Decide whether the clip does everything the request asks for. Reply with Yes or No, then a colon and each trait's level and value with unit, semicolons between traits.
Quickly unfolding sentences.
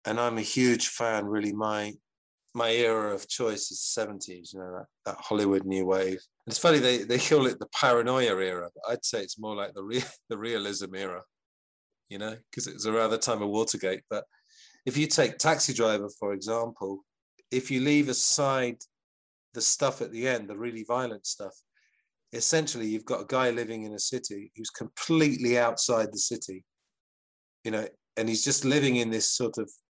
No: average, 190 wpm